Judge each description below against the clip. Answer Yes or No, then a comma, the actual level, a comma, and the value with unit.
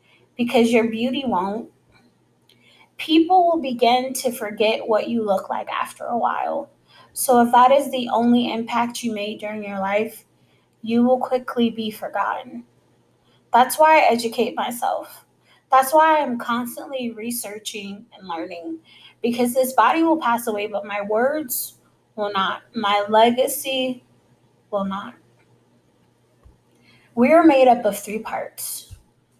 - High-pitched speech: Yes, high, 235 Hz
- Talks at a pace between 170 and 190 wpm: No, slow, 135 wpm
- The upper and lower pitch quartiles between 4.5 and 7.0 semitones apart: No, average, 3.4 semitones